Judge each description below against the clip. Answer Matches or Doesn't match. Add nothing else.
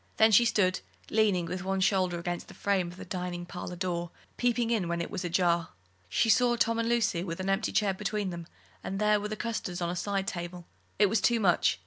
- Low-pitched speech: Doesn't match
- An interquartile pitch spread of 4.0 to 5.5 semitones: Doesn't match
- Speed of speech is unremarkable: Doesn't match